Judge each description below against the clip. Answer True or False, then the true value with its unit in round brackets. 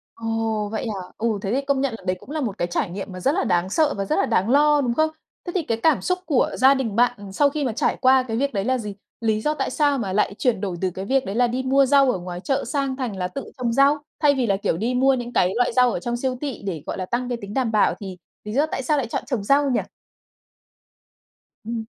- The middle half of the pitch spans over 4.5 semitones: True (5.0 semitones)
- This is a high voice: True (240 Hz)